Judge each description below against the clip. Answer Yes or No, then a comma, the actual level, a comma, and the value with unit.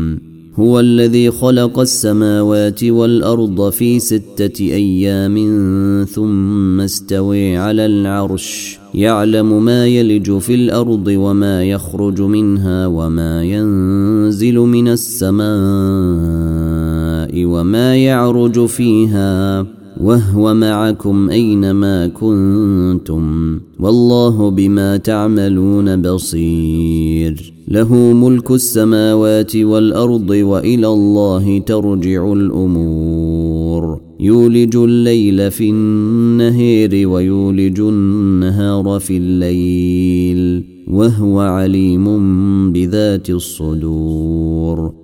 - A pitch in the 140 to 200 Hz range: No, low, 100 Hz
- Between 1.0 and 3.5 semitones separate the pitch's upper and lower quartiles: Yes, average, 3.0 semitones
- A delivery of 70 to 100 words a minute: Yes, average, 75 wpm